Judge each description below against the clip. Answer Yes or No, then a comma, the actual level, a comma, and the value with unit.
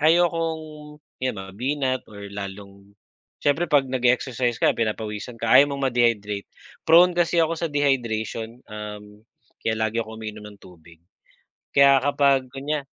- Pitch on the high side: No, low, 125 Hz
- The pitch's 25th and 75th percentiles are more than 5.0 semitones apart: Yes, wide, 5.4 semitones